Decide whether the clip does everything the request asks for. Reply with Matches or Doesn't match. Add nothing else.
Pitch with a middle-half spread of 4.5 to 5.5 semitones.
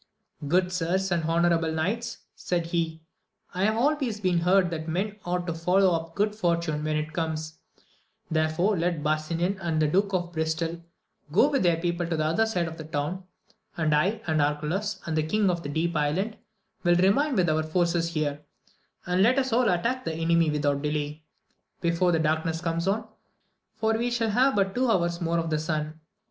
Doesn't match